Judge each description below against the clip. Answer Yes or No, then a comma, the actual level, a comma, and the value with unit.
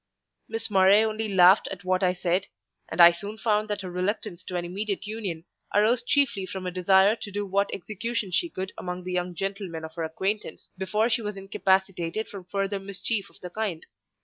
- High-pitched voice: Yes, high, 195 Hz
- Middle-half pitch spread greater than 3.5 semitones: No, narrow, 2.6 semitones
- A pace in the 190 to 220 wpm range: Yes, average, 200 wpm